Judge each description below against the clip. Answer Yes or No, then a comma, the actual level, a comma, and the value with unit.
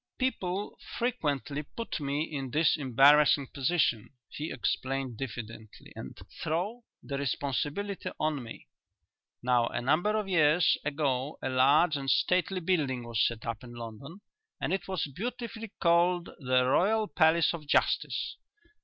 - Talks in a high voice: No, medium, 150 Hz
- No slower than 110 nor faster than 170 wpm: Yes, slow, 135 wpm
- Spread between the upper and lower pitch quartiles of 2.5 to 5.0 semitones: No, wide, 5.5 semitones